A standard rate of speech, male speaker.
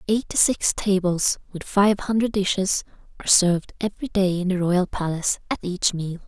No: average, 170 wpm; female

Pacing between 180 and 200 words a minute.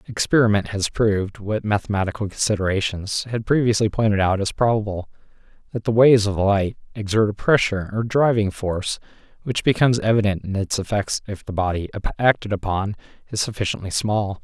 No: average, 155 wpm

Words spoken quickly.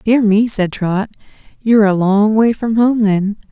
No: average, 190 wpm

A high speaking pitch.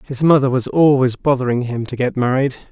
No: low, 130 Hz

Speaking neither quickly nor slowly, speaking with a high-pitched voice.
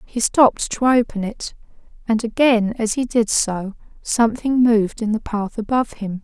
Yes: average, 175 wpm; high, 225 Hz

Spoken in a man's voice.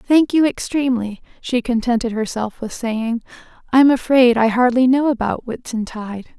No: female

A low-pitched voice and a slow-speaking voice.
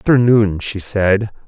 Yes: low, 105 Hz; slow, 120 wpm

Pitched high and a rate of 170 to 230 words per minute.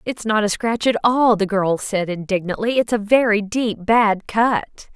Yes: high, 215 Hz; average, 195 wpm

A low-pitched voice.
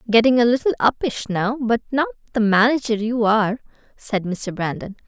No: high, 225 Hz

